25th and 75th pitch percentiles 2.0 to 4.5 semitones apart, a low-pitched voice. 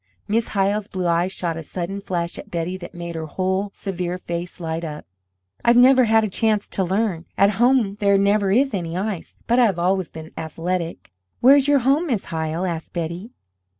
No: average, 4.0 semitones; high, 190 Hz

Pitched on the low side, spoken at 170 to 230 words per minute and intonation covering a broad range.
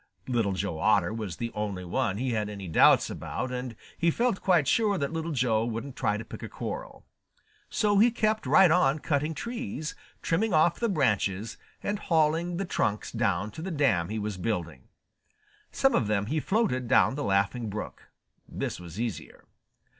Yes: low, 125 Hz; average, 180 wpm; wide, 8.2 semitones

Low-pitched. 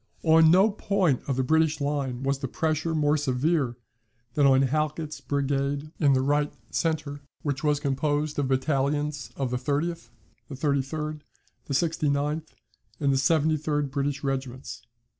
No: medium, 145 Hz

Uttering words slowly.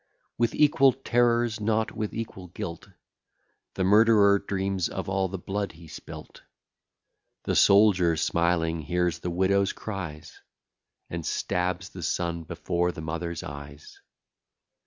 Yes: slow, 125 wpm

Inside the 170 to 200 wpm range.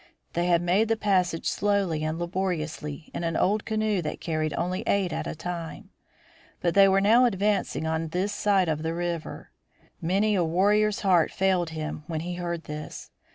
Yes: average, 180 wpm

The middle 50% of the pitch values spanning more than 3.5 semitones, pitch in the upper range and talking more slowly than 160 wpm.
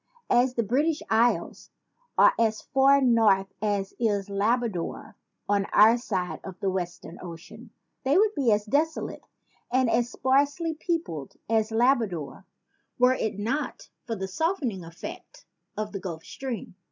Yes: average, 5.0 semitones; high, 225 Hz; average, 140 wpm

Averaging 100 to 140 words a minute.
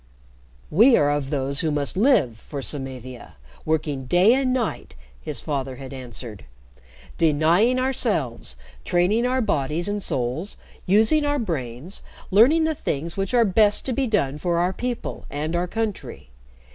No: average, 150 wpm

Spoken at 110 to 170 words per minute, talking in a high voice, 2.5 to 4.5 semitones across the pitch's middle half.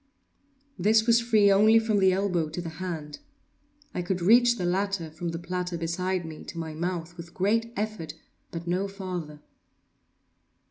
No: average, 165 wpm; medium, 180 Hz; average, 3.3 semitones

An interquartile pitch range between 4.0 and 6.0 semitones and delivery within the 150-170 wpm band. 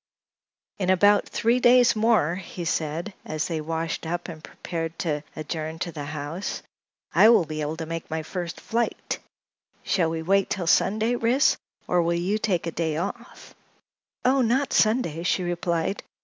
Yes: average, 4.8 semitones; average, 165 wpm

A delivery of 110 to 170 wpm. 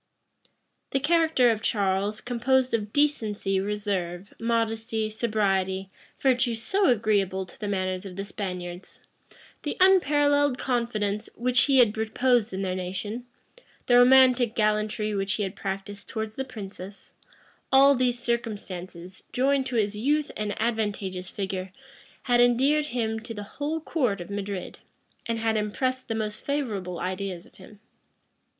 Yes: average, 140 wpm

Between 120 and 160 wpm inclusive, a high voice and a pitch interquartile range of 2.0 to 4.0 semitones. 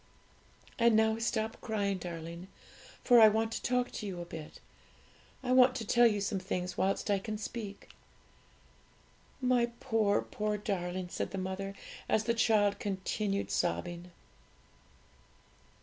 Yes: average, 140 wpm; high, 205 Hz; average, 3.1 semitones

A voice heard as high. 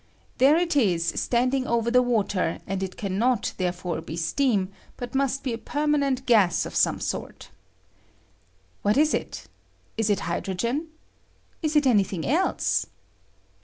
Yes: high, 235 Hz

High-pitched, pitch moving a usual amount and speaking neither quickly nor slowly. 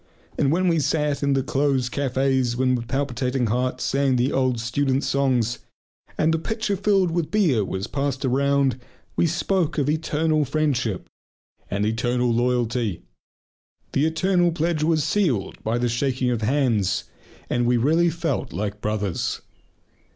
No: low, 135 Hz; average, 4.2 semitones; average, 150 wpm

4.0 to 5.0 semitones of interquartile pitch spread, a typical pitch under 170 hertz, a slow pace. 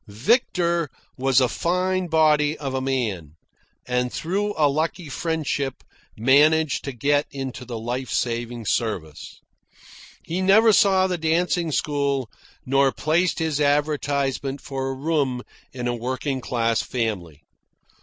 Yes: average, 4.4 semitones; medium, 140 Hz; slow, 130 wpm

